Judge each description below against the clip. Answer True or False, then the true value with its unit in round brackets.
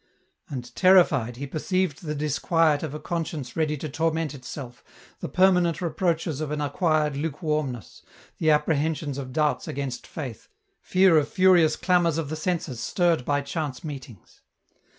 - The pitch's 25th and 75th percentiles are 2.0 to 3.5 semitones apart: True (2.8 semitones)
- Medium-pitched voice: True (155 Hz)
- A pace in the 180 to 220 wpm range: False (150 wpm)